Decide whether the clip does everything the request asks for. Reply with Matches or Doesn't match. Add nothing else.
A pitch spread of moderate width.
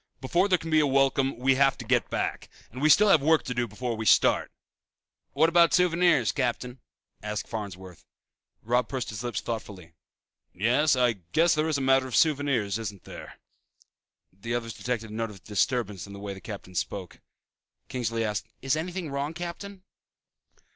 Doesn't match